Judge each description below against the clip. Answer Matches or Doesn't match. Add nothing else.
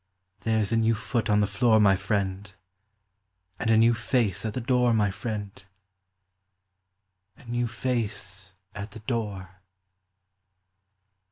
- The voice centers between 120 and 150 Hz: Doesn't match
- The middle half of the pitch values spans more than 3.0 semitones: Doesn't match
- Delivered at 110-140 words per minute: Matches